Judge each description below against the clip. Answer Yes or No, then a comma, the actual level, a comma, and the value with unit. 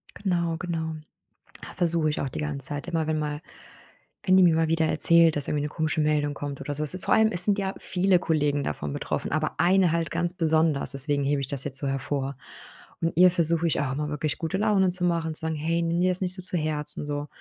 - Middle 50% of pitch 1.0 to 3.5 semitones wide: Yes, average, 2.9 semitones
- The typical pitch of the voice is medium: Yes, medium, 160 Hz